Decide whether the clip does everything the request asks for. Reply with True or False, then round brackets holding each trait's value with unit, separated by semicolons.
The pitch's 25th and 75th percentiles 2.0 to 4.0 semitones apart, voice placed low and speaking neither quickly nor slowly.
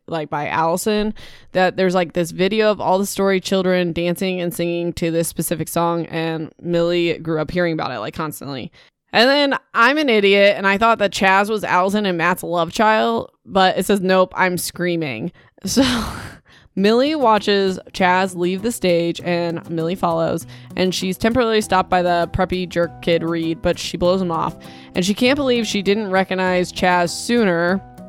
False (2.8 semitones; 180 Hz; 180 wpm)